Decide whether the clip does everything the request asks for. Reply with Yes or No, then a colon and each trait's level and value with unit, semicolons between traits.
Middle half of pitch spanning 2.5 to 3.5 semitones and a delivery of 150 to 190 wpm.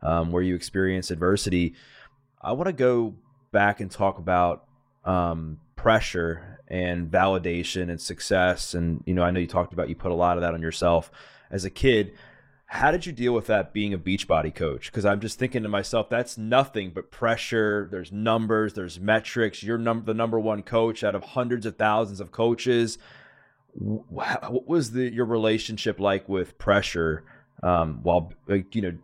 No: average, 4.2 semitones; average, 185 wpm